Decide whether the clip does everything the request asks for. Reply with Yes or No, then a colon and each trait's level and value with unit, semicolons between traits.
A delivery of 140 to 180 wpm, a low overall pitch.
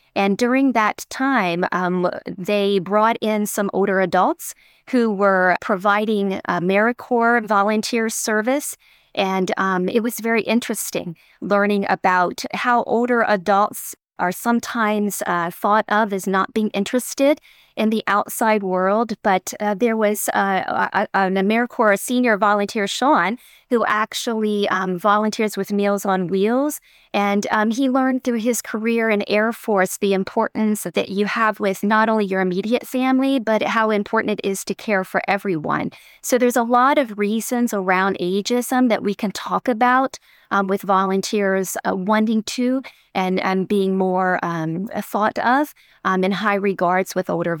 No: average, 155 wpm; high, 210 Hz